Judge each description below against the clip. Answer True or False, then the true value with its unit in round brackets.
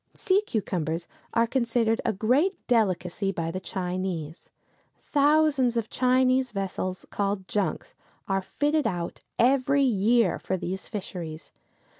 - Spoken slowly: True (120 wpm)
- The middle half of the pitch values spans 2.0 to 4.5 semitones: False (5.6 semitones)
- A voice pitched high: True (215 Hz)